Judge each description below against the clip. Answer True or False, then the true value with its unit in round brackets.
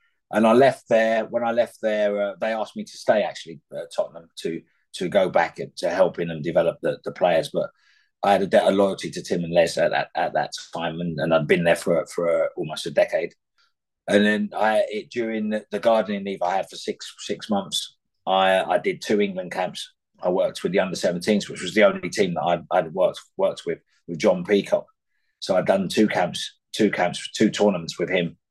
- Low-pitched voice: True (105 Hz)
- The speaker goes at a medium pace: False (230 wpm)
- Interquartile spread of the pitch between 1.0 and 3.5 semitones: True (2.8 semitones)